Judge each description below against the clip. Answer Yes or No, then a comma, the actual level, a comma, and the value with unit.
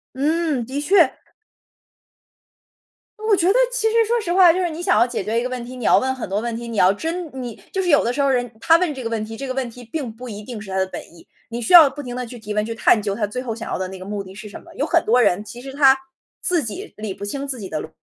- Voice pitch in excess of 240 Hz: Yes, very high, 250 Hz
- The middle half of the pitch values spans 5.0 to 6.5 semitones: Yes, wide, 5.6 semitones